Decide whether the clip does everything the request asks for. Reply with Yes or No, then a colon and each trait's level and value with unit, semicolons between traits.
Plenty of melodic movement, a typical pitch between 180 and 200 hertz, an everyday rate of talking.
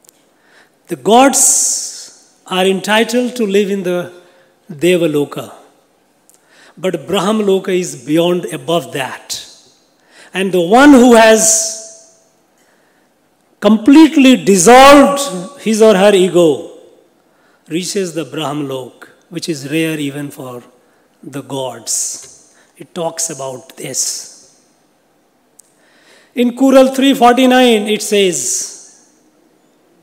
Yes: wide, 6.7 semitones; high, 190 Hz; average, 90 wpm